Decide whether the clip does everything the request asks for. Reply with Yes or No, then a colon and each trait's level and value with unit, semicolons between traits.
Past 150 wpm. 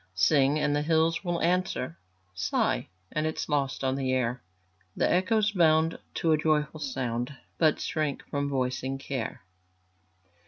No: average, 145 wpm